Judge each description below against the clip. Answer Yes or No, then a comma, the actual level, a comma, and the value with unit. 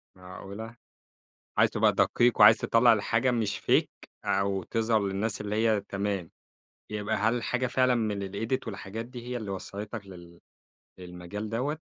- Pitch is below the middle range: Yes, low, 105 Hz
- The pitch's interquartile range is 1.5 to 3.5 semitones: Yes, average, 2.8 semitones